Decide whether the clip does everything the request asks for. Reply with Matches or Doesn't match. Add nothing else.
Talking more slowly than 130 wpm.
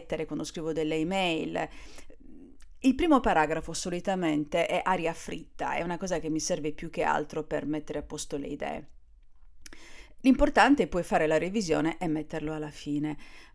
Doesn't match